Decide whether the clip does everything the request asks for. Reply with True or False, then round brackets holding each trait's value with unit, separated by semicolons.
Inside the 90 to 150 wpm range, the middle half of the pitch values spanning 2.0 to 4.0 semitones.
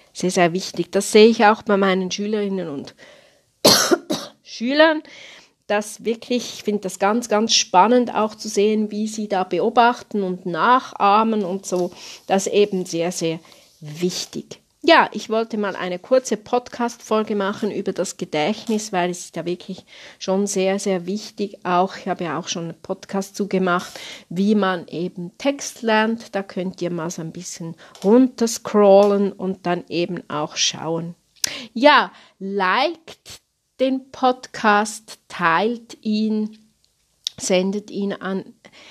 True (145 wpm; 3.5 semitones)